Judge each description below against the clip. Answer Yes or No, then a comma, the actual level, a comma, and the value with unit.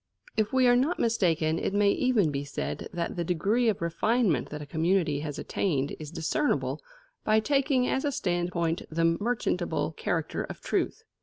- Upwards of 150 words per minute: Yes, average, 170 wpm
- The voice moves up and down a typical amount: No, wide, 6.0 semitones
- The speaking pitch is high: No, medium, 175 Hz